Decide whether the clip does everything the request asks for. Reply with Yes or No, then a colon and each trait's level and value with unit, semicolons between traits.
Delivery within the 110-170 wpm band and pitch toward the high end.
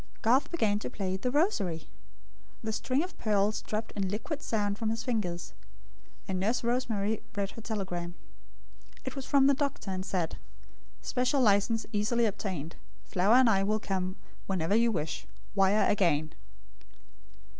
Yes: average, 150 wpm; high, 210 Hz